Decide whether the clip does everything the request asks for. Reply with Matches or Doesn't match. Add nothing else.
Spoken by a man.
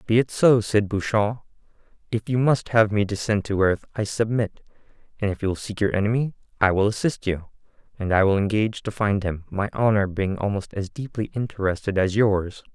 Matches